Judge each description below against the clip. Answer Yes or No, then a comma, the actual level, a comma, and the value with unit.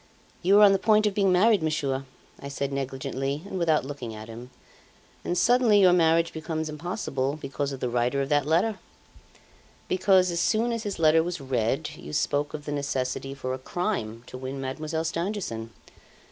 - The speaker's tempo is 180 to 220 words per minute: Yes, average, 185 wpm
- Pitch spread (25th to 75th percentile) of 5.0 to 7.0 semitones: Yes, wide, 5.4 semitones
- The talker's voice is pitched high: No, medium, 155 Hz